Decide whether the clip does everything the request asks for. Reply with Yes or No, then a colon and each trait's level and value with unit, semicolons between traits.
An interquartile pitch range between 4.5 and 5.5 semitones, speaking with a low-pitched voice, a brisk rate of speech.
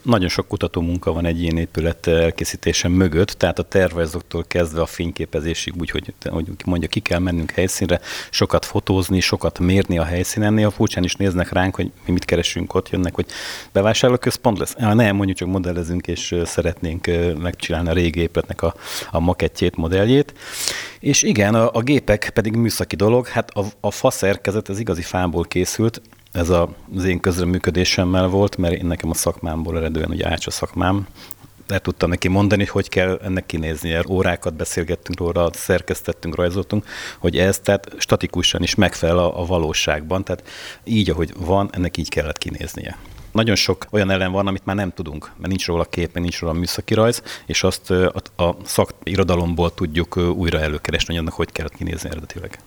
No: narrow, 2.4 semitones; very low, 90 Hz; fast, 175 wpm